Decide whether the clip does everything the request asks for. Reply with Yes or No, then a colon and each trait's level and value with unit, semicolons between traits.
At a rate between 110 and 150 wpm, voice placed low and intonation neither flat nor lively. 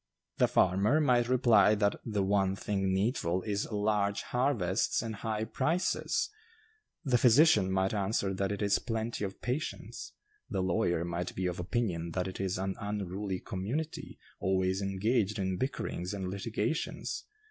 Yes: average, 145 wpm; low, 100 Hz; average, 3.3 semitones